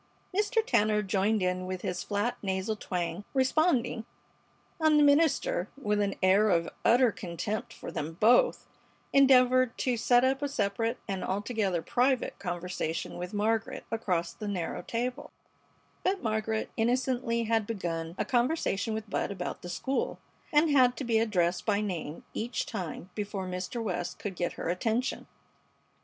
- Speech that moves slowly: No, average, 150 wpm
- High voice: Yes, high, 215 Hz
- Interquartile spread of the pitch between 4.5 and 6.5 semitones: Yes, average, 5.1 semitones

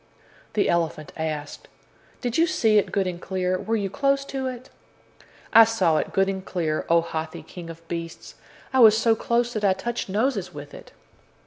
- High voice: Yes, high, 195 Hz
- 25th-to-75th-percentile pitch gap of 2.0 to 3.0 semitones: No, wide, 5.5 semitones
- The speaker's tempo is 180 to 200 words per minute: Yes, average, 190 wpm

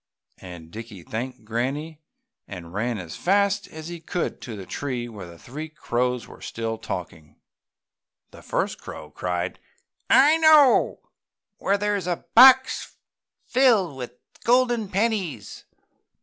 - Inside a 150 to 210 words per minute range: No, slow, 135 wpm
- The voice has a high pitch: No, medium, 145 Hz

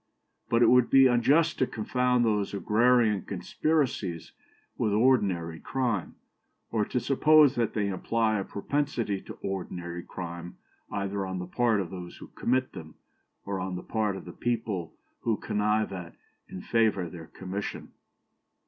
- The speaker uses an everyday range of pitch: Yes, average, 4.6 semitones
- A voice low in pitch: Yes, low, 105 Hz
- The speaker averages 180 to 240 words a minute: No, average, 150 wpm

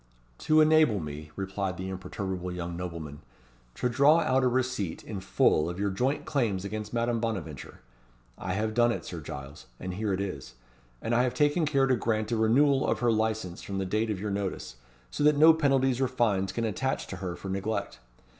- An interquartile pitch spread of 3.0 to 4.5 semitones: No, wide, 5.4 semitones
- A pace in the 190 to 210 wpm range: Yes, average, 200 wpm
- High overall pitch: No, low, 110 Hz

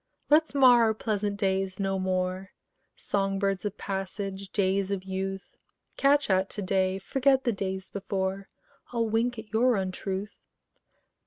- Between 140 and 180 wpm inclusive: Yes, average, 145 wpm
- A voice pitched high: Yes, high, 195 Hz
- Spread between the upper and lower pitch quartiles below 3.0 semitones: Yes, narrow, 2.4 semitones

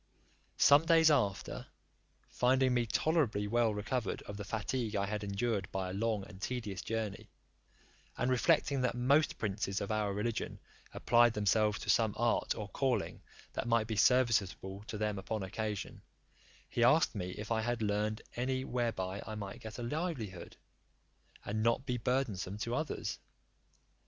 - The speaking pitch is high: No, low, 110 Hz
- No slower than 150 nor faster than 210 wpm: Yes, average, 155 wpm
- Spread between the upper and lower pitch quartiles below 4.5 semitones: Yes, average, 3.3 semitones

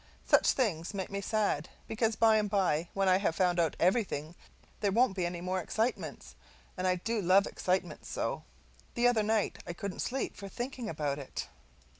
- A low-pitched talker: No, high, 195 Hz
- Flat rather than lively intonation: No, average, 3.8 semitones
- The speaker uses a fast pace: No, average, 185 wpm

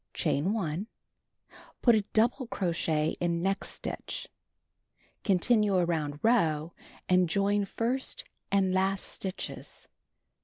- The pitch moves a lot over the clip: No, average, 4.0 semitones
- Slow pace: Yes, slow, 105 wpm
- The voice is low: No, high, 190 Hz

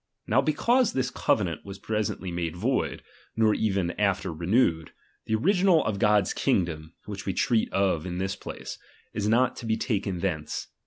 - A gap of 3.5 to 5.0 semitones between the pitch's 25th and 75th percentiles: Yes, average, 4.2 semitones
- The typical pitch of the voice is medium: No, low, 100 Hz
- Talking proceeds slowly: No, average, 165 wpm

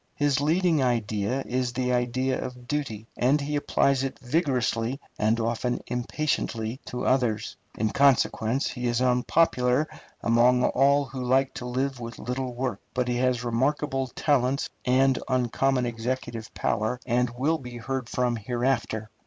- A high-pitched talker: No, low, 125 Hz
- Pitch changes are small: Yes, narrow, 2.1 semitones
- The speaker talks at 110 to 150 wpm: Yes, average, 145 wpm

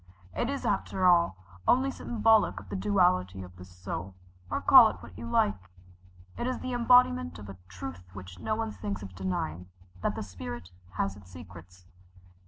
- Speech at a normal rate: Yes, average, 180 wpm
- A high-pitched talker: No, very low, 95 Hz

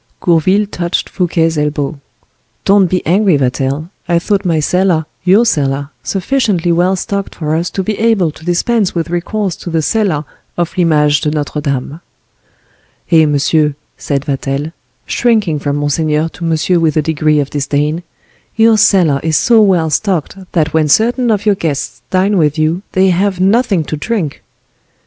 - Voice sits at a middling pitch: Yes, medium, 165 Hz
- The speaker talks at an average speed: Yes, average, 160 wpm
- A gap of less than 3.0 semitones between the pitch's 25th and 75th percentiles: No, average, 4.3 semitones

